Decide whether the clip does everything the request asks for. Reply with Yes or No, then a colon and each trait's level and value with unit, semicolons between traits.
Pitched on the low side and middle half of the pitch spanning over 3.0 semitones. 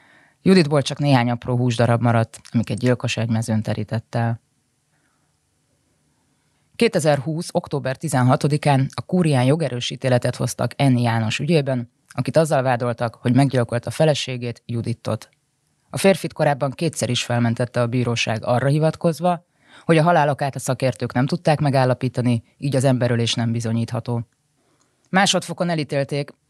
Yes: low, 130 Hz; average, 3.7 semitones